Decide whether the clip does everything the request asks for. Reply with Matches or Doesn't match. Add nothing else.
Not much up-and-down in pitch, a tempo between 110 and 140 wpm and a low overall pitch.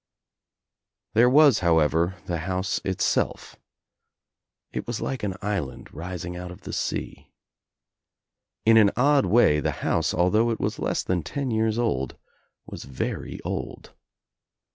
Doesn't match